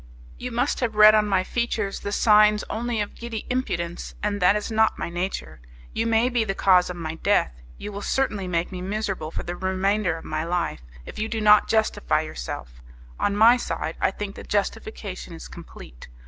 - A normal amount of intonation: Yes, average, 3.6 semitones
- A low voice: No, high, 205 Hz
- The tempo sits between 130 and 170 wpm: No, average, 200 wpm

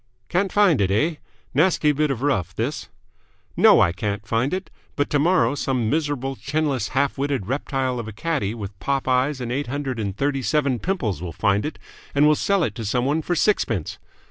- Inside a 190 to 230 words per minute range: Yes, average, 195 wpm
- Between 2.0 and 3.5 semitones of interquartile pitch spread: No, average, 4.9 semitones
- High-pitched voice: No, low, 135 Hz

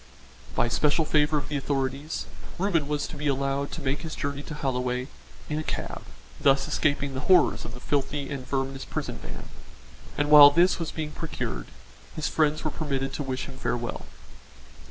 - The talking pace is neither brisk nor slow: Yes, average, 180 wpm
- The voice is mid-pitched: Yes, medium, 145 Hz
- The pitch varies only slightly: Yes, narrow, 2.0 semitones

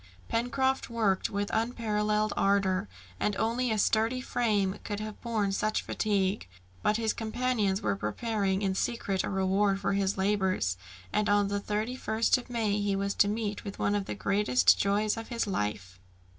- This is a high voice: Yes, high, 205 Hz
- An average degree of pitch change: No, narrow, 2.2 semitones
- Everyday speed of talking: Yes, average, 170 wpm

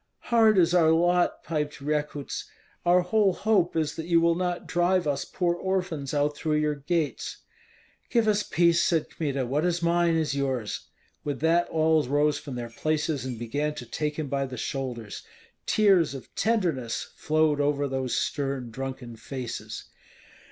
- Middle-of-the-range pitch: Yes, medium, 150 Hz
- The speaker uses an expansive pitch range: No, average, 3.9 semitones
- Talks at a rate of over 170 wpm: No, average, 165 wpm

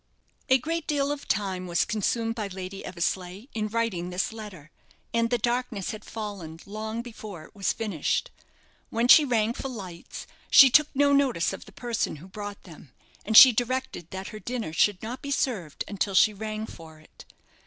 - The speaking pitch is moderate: No, high, 215 Hz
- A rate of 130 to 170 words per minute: No, average, 185 wpm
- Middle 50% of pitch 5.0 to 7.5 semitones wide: No, average, 4.4 semitones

